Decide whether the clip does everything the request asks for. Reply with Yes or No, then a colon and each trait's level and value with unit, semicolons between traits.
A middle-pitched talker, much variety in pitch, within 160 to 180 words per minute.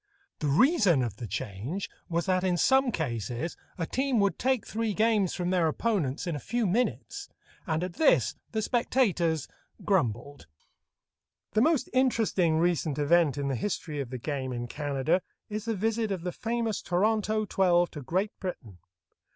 Yes: medium, 180 Hz; wide, 7.0 semitones; average, 165 wpm